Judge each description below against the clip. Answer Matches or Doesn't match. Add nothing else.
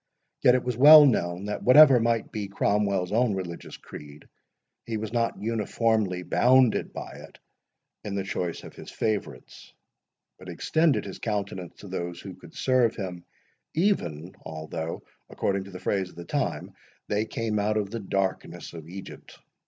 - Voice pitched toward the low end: Matches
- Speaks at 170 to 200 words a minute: Doesn't match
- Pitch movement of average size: Matches